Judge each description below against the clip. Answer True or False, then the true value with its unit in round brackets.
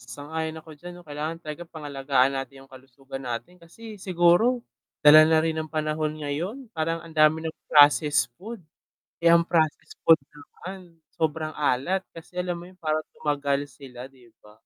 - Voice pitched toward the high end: False (155 Hz)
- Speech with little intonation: False (3.0 semitones)